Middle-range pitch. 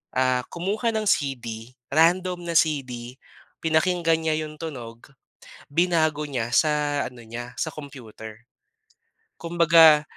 Yes: medium, 150 Hz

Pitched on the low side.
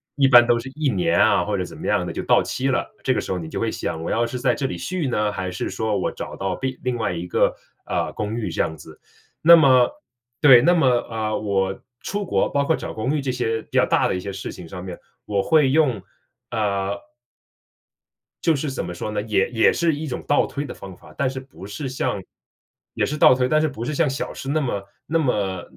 Yes: low, 120 Hz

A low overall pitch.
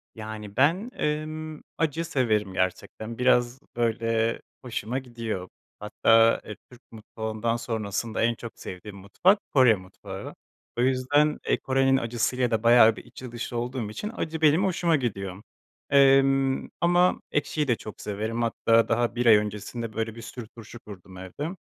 Yes: low, 115 Hz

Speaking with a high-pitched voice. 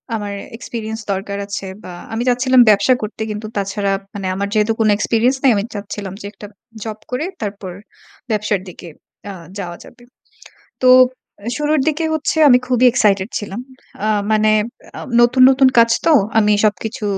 Yes: high, 215 Hz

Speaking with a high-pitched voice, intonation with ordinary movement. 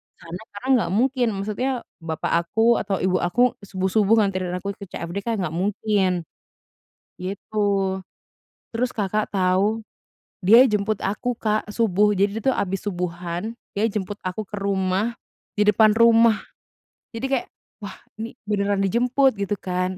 Yes: high, 205 Hz; average, 3.0 semitones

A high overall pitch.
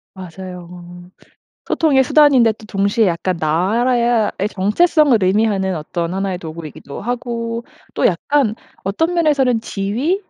Yes: high, 210 Hz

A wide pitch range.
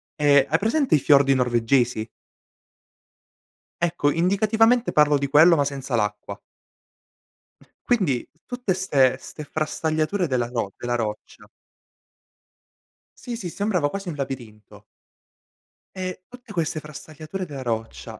Yes: wide, 6.1 semitones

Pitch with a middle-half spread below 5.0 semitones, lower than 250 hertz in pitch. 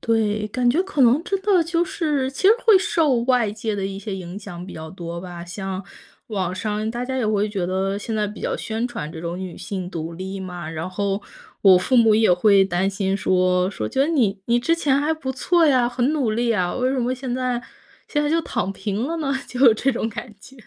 No: wide, 5.6 semitones; high, 215 Hz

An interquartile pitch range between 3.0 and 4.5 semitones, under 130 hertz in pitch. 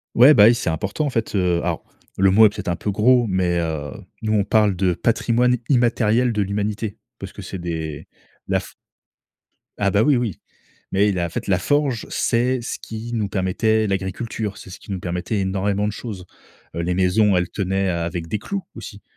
Yes: average, 3.7 semitones; low, 100 Hz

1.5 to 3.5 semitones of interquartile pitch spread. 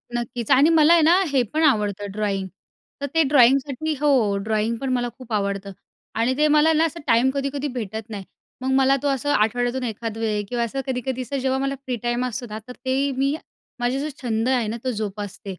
No: average, 3.9 semitones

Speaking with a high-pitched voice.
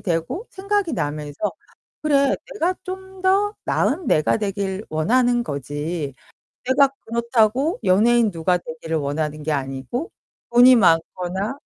Yes: high, 210 Hz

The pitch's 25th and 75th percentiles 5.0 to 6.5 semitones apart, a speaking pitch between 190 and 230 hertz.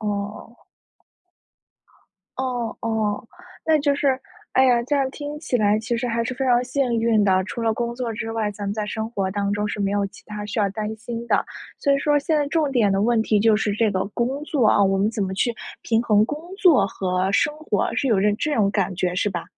No: average, 3.7 semitones; high, 225 Hz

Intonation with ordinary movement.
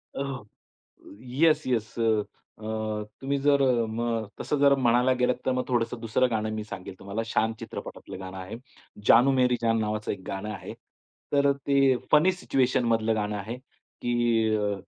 Yes: average, 3.2 semitones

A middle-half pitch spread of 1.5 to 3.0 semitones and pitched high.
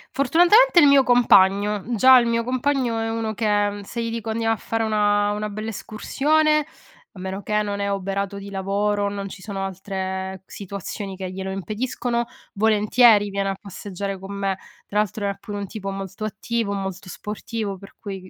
Yes: narrow, 2.6 semitones; high, 205 Hz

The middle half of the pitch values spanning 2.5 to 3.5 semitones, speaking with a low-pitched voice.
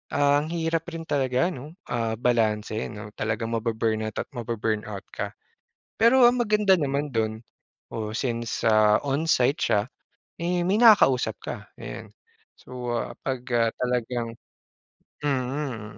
No: average, 4.9 semitones; low, 125 Hz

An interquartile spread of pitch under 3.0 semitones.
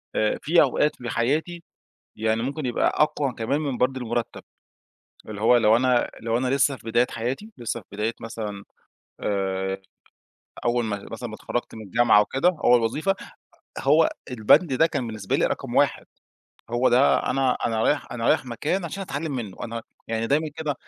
No: average, 3.9 semitones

